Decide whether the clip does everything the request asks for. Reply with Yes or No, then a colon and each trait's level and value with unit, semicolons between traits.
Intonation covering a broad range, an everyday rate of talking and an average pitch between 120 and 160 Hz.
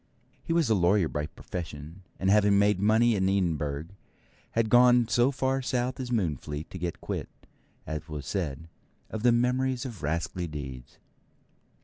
No: wide, 7.3 semitones; average, 155 wpm; low, 100 Hz